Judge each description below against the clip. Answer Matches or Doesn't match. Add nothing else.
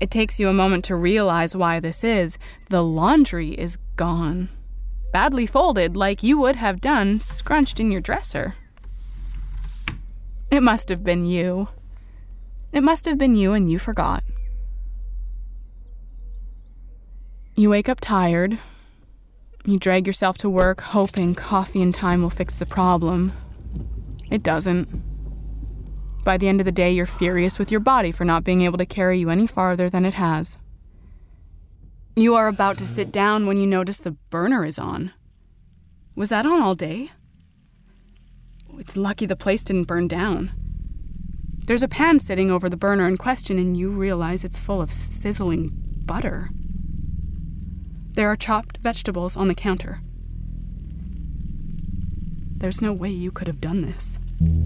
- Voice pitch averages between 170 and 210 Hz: Matches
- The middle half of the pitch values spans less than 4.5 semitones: Matches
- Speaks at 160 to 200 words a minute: Doesn't match